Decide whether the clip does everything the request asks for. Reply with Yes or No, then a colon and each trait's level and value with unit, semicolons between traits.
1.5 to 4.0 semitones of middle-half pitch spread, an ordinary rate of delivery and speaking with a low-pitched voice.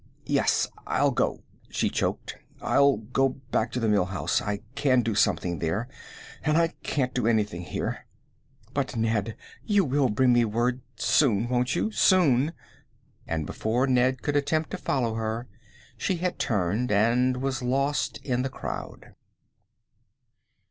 Yes: average, 3.7 semitones; average, 150 wpm; low, 125 Hz